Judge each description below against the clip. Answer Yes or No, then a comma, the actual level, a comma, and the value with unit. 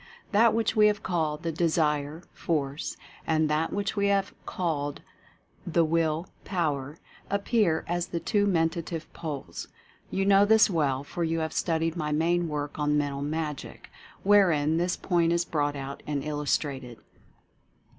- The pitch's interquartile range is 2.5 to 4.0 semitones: Yes, average, 3.1 semitones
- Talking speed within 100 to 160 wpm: Yes, average, 150 wpm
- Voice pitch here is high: No, medium, 165 Hz